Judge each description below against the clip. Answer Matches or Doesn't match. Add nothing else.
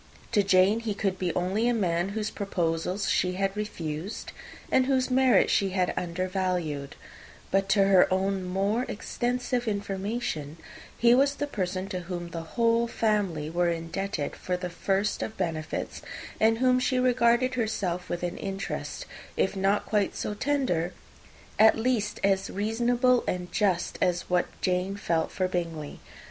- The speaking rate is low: Doesn't match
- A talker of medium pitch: Doesn't match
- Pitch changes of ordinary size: Matches